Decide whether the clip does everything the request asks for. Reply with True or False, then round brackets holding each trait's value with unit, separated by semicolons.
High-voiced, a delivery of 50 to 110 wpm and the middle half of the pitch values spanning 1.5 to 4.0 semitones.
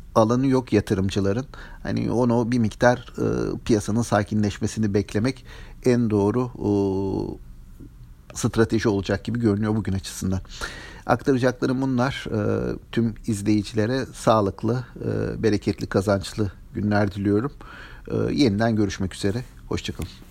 False (105 Hz; 105 wpm; 3.1 semitones)